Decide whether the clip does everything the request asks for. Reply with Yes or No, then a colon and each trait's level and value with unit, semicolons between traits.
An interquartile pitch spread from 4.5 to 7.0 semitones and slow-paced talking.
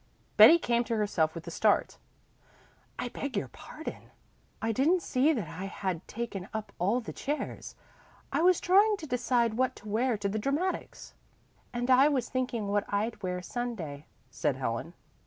No: average, 4.8 semitones; average, 170 wpm